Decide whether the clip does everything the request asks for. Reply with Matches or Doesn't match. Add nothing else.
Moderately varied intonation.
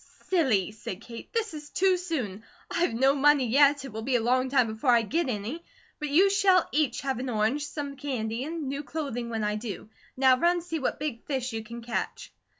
Matches